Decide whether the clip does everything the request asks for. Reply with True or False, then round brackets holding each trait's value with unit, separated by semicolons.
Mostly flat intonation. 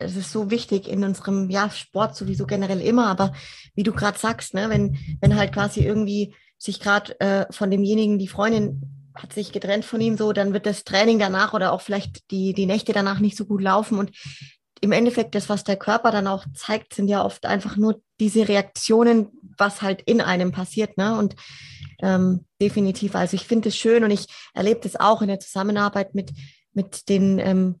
True (1.9 semitones)